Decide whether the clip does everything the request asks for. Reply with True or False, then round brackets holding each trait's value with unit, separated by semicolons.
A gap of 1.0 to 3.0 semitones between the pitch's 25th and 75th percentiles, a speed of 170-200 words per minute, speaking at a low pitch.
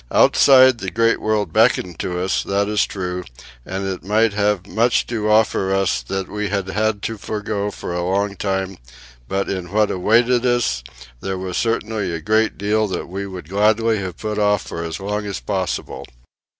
True (2.4 semitones; 185 wpm; 100 Hz)